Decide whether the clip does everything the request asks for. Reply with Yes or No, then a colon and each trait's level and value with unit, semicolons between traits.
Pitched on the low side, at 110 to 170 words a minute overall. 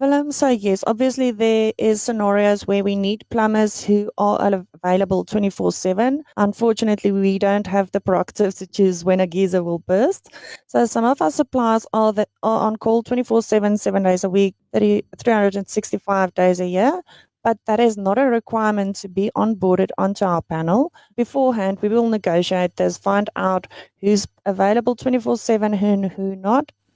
No: high, 205 Hz; average, 165 wpm